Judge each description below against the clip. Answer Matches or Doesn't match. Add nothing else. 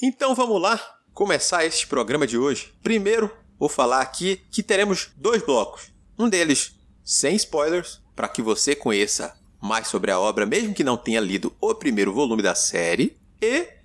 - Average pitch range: Doesn't match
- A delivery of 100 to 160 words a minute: Doesn't match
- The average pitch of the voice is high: Matches